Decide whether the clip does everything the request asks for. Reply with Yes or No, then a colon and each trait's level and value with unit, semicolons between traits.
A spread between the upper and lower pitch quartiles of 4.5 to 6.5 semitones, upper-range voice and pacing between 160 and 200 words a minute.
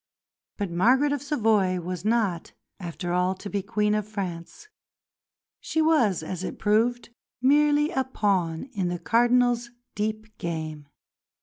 No: average, 5.2 semitones; high, 210 Hz; slow, 135 wpm